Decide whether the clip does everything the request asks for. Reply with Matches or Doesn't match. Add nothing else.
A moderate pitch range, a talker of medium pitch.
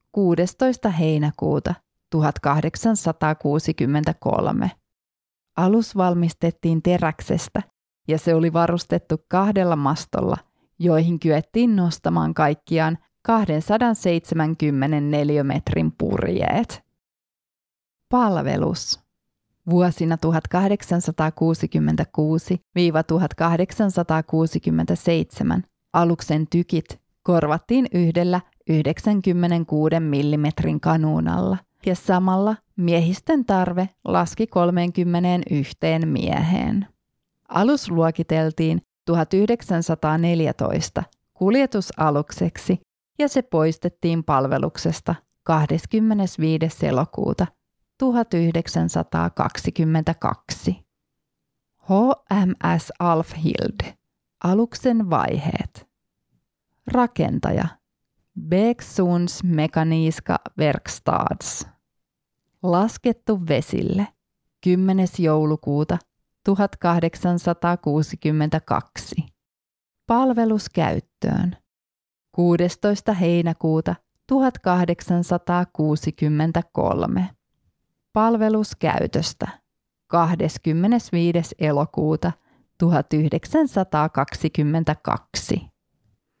Matches